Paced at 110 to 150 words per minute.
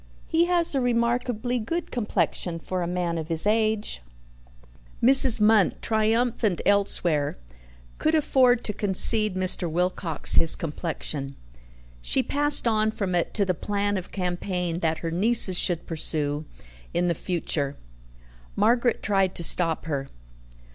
Yes: slow, 135 wpm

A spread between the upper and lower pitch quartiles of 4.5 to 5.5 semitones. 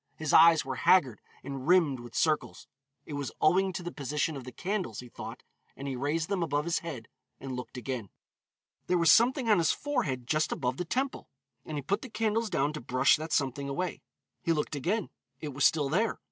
Yes: average, 5.1 semitones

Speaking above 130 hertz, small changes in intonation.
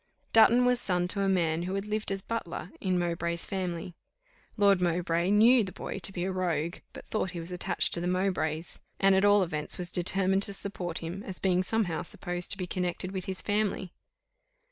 Yes: medium, 185 Hz; narrow, 2.1 semitones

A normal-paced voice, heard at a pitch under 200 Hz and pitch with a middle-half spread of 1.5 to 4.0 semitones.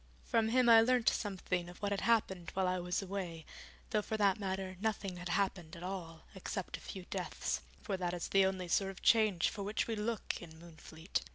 No: fast, 210 wpm; high, 190 Hz; average, 2.9 semitones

